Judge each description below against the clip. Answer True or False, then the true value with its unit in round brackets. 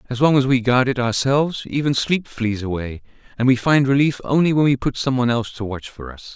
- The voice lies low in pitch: True (125 Hz)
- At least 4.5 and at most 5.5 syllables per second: False (5.8 syllables/s)